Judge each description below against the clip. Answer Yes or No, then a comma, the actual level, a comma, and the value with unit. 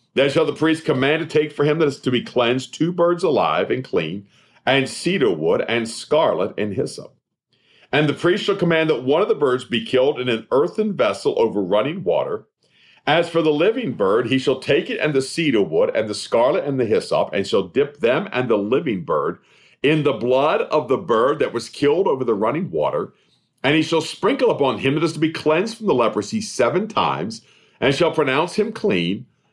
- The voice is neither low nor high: Yes, medium, 160 Hz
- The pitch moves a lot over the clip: Yes, wide, 7.6 semitones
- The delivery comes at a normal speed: No, fast, 215 wpm